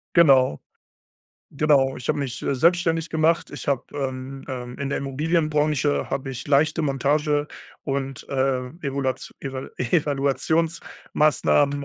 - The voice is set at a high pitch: No, medium, 140 Hz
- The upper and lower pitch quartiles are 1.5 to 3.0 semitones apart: Yes, narrow, 2.4 semitones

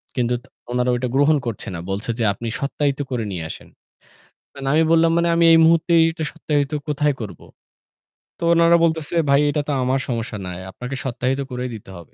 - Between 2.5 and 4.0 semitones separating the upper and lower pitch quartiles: No, average, 4.7 semitones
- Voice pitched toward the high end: No, low, 135 Hz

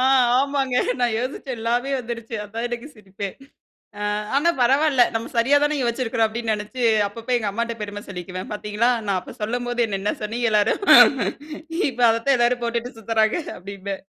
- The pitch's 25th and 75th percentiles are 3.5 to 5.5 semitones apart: No, average, 2.8 semitones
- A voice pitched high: Yes, high, 230 Hz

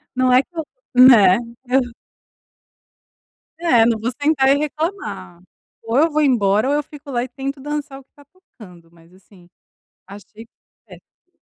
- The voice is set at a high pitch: Yes, very high, 260 Hz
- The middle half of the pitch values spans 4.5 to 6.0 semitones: Yes, wide, 5.5 semitones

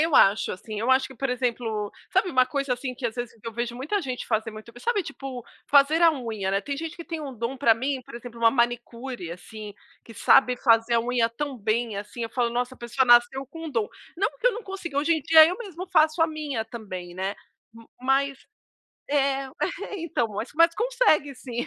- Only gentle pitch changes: No, average, 4.1 semitones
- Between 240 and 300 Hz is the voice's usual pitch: Yes, very high, 250 Hz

